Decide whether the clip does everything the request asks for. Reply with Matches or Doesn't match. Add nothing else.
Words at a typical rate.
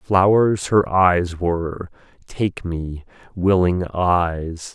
Doesn't match